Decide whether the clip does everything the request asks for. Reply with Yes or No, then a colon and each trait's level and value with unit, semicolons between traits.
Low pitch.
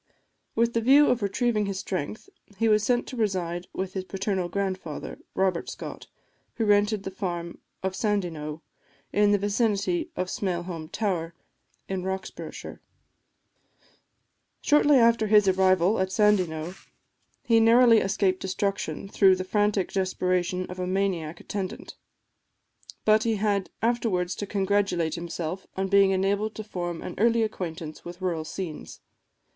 No: high, 195 Hz